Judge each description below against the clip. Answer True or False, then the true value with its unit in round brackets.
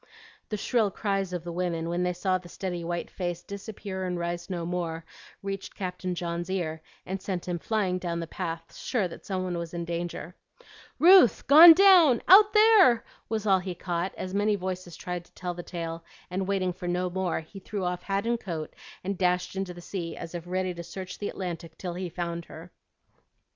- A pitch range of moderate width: False (2.2 semitones)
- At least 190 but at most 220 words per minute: True (205 wpm)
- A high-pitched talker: False (180 Hz)